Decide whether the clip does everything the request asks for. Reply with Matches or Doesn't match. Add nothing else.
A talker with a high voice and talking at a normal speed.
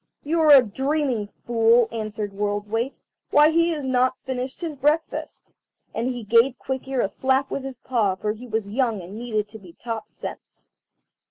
Matches